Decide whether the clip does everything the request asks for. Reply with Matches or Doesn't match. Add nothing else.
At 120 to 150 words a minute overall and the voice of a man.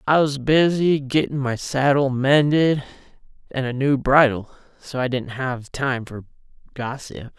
Matches